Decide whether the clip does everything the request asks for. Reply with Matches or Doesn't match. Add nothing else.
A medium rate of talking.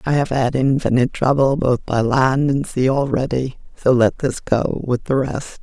Matches